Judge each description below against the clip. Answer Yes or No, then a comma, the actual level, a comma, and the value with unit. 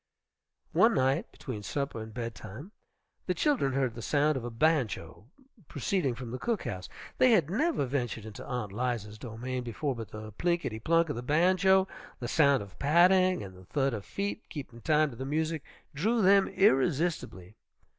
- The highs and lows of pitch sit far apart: Yes, wide, 6.7 semitones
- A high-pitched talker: No, low, 135 Hz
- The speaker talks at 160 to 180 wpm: Yes, average, 175 wpm